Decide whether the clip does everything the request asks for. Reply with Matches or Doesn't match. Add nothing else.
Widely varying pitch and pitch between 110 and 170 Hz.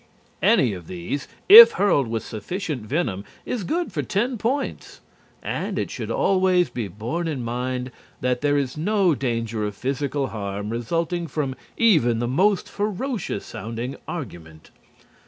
Matches